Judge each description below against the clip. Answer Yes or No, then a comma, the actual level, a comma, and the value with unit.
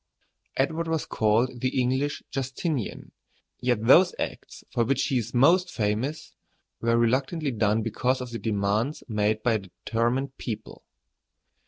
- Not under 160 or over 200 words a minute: No, average, 145 wpm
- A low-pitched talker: Yes, low, 125 Hz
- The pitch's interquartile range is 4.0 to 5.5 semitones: No, average, 3.5 semitones